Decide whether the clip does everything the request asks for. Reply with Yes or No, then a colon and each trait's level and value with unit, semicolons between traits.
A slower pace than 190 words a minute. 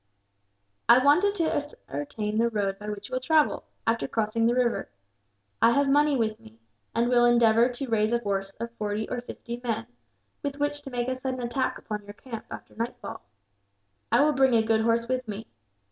No: average, 195 wpm